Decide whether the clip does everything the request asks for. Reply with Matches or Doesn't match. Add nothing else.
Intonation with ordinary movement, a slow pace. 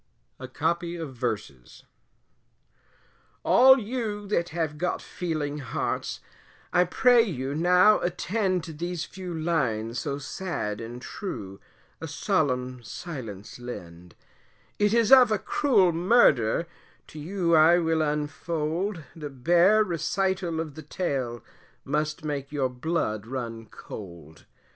Doesn't match